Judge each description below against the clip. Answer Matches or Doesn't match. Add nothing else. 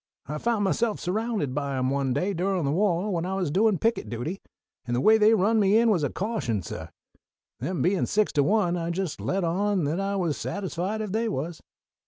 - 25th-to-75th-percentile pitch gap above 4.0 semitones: Matches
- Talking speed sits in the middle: Doesn't match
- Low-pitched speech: Doesn't match